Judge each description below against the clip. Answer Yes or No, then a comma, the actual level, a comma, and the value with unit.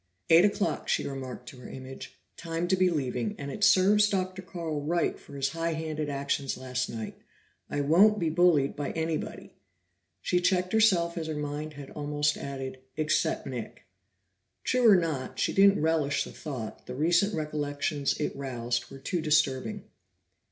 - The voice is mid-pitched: Yes, medium, 155 Hz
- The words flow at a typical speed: Yes, average, 165 wpm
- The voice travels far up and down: No, average, 4.2 semitones